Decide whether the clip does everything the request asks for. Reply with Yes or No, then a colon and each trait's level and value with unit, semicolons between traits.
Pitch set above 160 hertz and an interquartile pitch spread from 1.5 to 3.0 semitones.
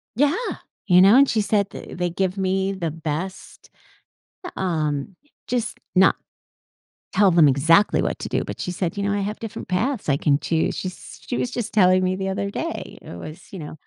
No: medium, 185 Hz; average, 3.4 semitones